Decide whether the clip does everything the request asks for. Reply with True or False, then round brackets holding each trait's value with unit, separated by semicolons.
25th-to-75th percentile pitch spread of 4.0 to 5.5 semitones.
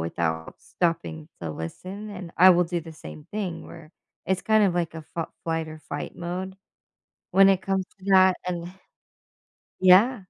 False (2.8 semitones)